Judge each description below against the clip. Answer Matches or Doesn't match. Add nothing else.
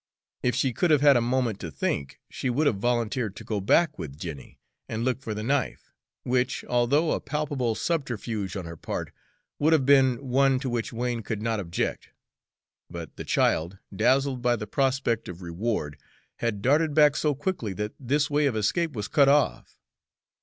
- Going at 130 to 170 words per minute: Doesn't match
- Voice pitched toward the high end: Doesn't match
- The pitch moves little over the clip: Doesn't match